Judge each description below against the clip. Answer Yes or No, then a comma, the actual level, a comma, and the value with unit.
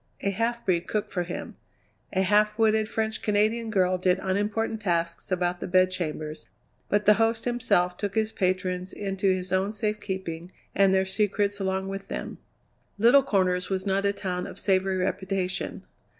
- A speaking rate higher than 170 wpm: No, average, 165 wpm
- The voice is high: Yes, high, 195 Hz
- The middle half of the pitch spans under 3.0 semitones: Yes, narrow, 2.4 semitones